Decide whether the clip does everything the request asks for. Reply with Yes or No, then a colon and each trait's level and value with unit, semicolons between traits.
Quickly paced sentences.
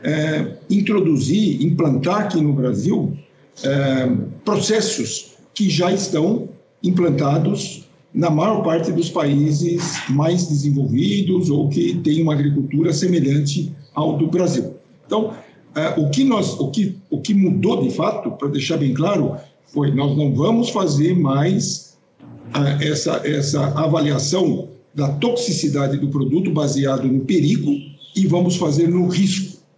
No: average, 135 wpm